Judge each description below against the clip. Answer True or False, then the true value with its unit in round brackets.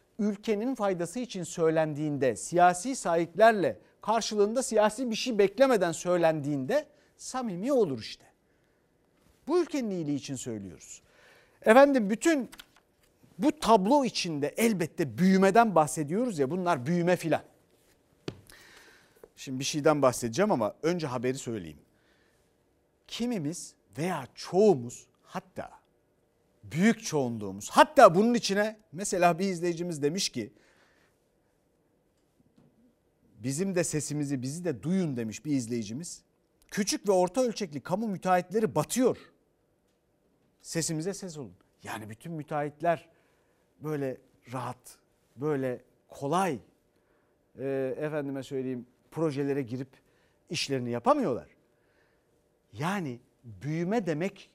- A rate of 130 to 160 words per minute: False (100 wpm)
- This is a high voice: False (165 Hz)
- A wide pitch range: True (7.1 semitones)